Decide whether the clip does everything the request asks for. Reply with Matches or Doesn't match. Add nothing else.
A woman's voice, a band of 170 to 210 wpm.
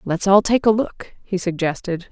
Matches